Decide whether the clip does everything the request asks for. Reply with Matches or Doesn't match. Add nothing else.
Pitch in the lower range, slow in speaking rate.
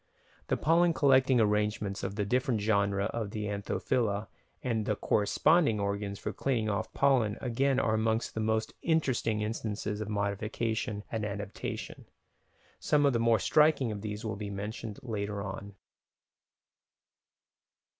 Doesn't match